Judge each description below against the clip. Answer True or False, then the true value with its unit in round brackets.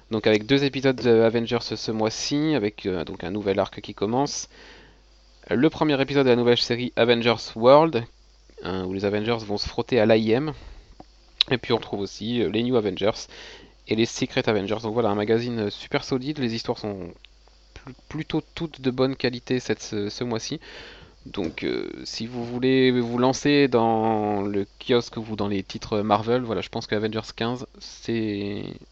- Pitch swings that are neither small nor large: True (3.6 semitones)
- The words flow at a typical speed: True (180 wpm)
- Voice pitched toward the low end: True (115 Hz)